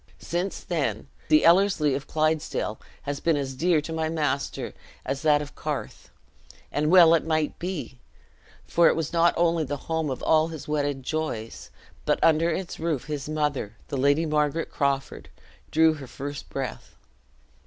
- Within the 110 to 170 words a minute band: Yes, average, 165 wpm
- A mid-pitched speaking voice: Yes, medium, 155 Hz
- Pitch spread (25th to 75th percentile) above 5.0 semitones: No, narrow, 2.5 semitones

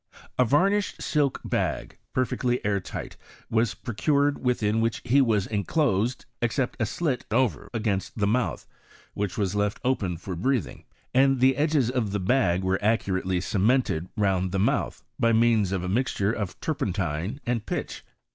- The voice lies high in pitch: No, low, 110 Hz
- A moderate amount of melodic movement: Yes, average, 4.7 semitones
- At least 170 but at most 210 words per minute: No, average, 155 wpm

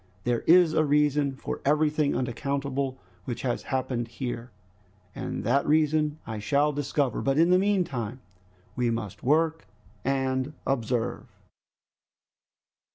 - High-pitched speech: No, medium, 140 Hz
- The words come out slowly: Yes, slow, 120 wpm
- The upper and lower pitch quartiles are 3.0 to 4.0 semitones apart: Yes, average, 3.3 semitones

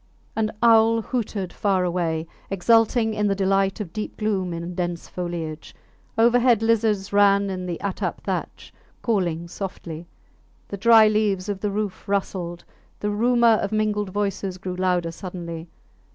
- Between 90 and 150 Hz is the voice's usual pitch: No, high, 195 Hz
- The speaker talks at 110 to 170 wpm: Yes, average, 145 wpm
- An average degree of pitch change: Yes, average, 3.2 semitones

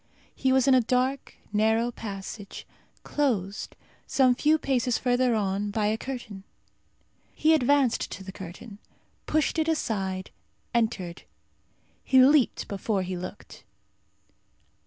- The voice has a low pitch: No, high, 230 Hz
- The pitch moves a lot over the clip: No, average, 4.8 semitones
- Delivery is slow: Yes, slow, 120 wpm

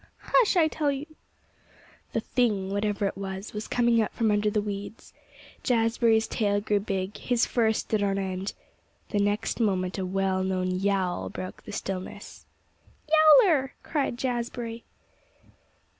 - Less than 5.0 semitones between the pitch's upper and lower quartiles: Yes, average, 3.6 semitones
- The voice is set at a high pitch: Yes, high, 210 Hz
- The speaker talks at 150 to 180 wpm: No, average, 140 wpm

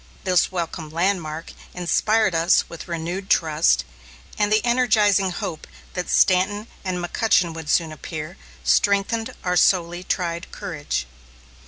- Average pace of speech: No, slow, 125 wpm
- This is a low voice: No, medium, 180 Hz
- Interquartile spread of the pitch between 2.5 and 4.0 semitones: Yes, average, 3.3 semitones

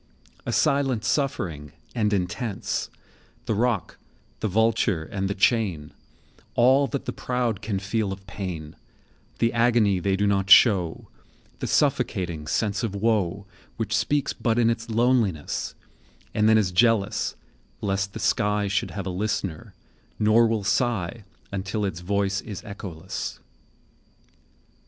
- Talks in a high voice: No, low, 105 Hz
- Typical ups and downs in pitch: Yes, average, 3.0 semitones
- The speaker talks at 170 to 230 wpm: No, slow, 135 wpm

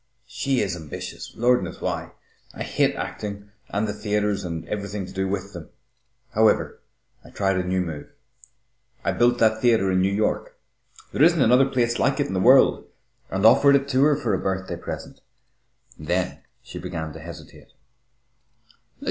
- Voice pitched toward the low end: Yes, low, 100 Hz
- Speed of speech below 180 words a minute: Yes, average, 170 wpm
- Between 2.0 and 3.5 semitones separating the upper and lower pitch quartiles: No, average, 4.7 semitones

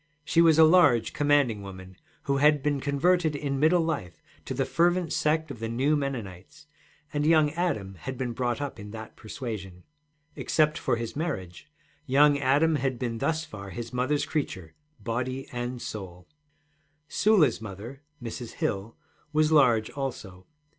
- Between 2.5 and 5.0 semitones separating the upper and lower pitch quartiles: No, wide, 5.4 semitones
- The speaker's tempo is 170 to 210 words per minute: No, average, 155 wpm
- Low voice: Yes, low, 130 Hz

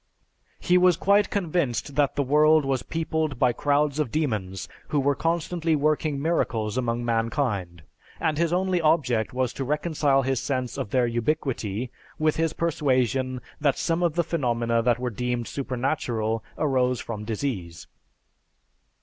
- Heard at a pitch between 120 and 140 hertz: Yes, low, 135 Hz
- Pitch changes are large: No, average, 4.6 semitones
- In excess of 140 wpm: Yes, average, 150 wpm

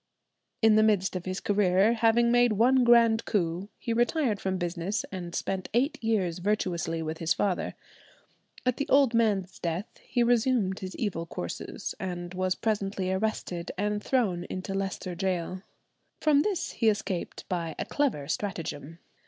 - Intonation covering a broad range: No, average, 4.2 semitones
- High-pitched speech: Yes, high, 195 Hz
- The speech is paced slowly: No, average, 155 wpm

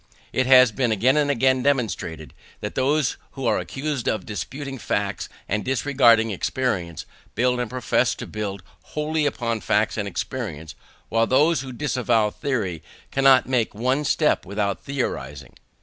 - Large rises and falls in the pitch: No, average, 4.2 semitones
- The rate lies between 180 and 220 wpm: No, average, 150 wpm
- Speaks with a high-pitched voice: No, low, 125 Hz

